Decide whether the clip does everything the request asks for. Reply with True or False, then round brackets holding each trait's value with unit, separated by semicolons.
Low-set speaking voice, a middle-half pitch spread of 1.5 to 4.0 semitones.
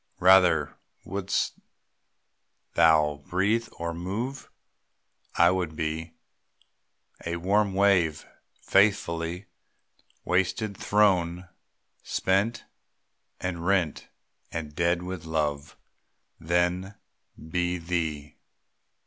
True (90 Hz; 2.7 semitones)